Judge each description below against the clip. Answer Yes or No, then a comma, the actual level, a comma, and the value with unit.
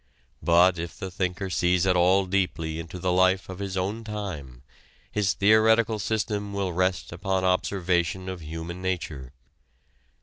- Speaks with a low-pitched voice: Yes, very low, 95 Hz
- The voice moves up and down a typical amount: No, narrow, 2.2 semitones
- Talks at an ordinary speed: Yes, average, 145 wpm